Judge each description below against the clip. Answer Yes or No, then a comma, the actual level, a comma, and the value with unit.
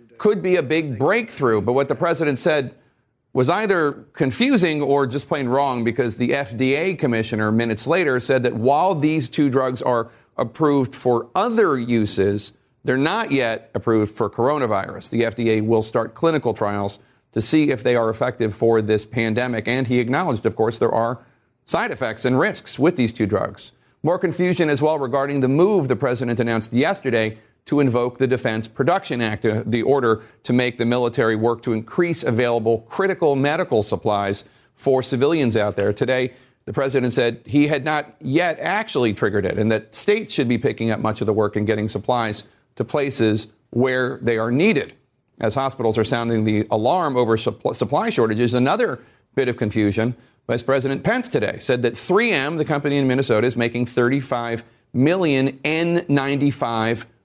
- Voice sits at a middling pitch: No, low, 125 Hz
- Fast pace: No, average, 175 wpm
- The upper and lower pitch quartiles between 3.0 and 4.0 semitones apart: Yes, average, 3.6 semitones